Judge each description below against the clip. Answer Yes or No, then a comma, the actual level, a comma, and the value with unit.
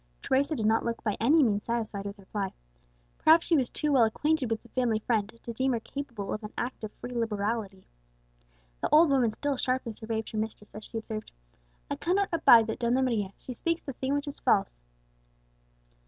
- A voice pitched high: Yes, high, 235 Hz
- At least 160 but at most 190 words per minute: No, fast, 205 wpm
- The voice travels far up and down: No, average, 3.8 semitones